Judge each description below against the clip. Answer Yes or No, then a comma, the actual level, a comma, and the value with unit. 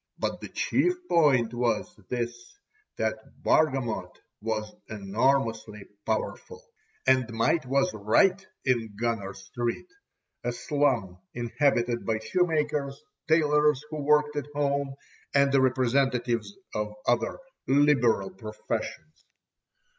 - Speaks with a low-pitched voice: Yes, low, 130 Hz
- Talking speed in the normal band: No, slow, 105 wpm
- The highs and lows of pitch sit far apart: No, average, 4.5 semitones